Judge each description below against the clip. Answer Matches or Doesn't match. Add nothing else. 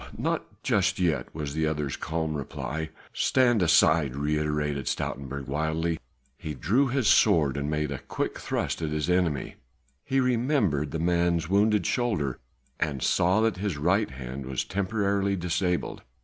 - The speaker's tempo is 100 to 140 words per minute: Doesn't match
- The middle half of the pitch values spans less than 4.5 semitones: Doesn't match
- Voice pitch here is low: Matches